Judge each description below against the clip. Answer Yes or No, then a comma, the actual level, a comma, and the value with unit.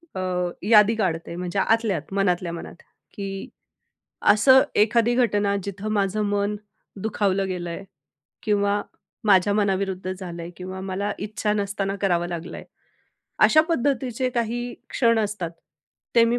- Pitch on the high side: Yes, high, 200 Hz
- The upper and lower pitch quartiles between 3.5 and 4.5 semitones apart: No, average, 2.8 semitones